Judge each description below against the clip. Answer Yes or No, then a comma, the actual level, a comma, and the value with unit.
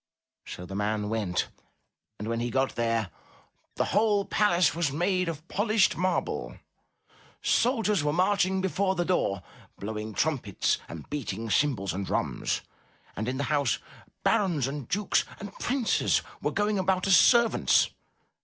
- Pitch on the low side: No, medium, 155 Hz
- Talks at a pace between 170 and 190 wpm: No, average, 145 wpm